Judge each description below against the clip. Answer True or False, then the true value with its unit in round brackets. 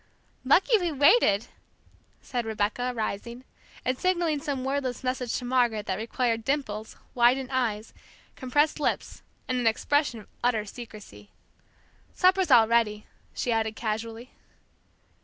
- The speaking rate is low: True (125 wpm)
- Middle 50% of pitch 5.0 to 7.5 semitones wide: False (3.4 semitones)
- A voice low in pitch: False (245 Hz)